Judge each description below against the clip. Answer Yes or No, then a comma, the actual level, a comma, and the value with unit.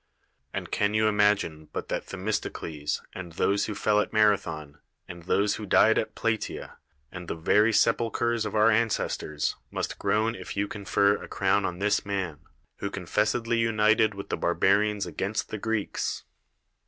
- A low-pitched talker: Yes, low, 105 Hz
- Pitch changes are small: Yes, narrow, 2.3 semitones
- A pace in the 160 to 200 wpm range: Yes, average, 165 wpm